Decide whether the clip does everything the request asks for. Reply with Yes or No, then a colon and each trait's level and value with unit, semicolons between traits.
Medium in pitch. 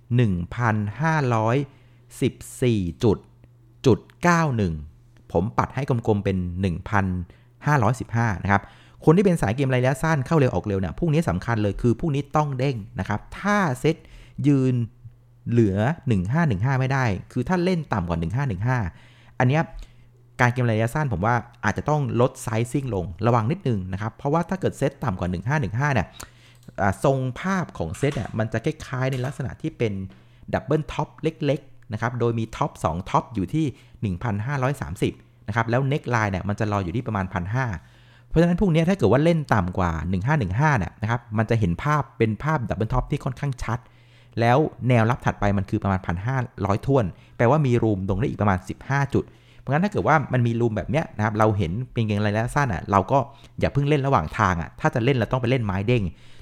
No: low, 120 Hz